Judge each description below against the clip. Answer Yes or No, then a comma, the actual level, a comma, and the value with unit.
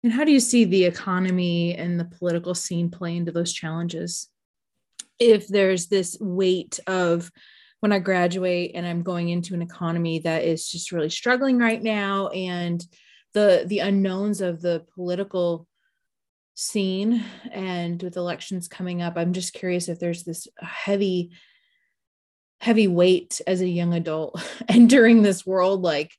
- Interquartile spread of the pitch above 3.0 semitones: No, average, 2.7 semitones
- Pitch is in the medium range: Yes, medium, 180 Hz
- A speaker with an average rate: Yes, average, 150 wpm